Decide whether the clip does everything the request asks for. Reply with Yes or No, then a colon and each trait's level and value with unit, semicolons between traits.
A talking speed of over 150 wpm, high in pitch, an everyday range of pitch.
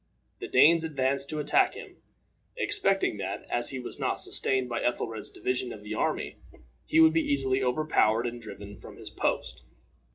No: average, 170 wpm; low, 130 Hz; average, 4.4 semitones